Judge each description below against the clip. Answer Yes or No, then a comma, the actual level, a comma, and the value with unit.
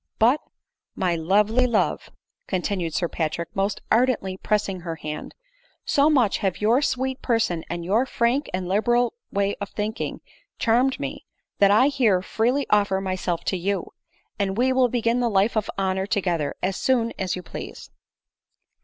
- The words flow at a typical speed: Yes, average, 170 wpm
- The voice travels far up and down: No, average, 4.4 semitones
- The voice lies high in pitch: Yes, high, 205 Hz